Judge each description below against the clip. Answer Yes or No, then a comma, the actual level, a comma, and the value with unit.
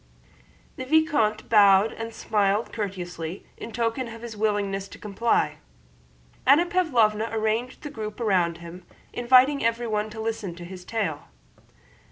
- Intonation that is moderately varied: Yes, average, 3.1 semitones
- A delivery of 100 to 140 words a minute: Yes, slow, 135 wpm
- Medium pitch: No, high, 220 Hz